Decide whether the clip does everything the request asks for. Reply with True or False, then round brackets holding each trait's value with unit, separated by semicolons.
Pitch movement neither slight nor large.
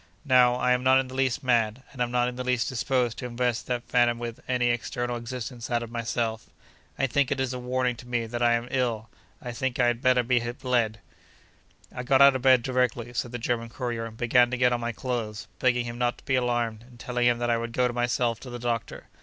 False (1.2 semitones)